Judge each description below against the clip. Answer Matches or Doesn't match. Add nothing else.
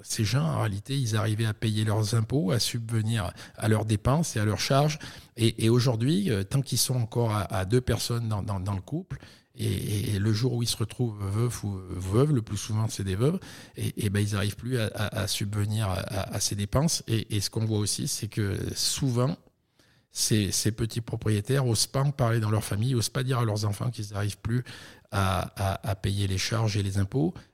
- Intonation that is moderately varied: Matches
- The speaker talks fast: Matches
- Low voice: Matches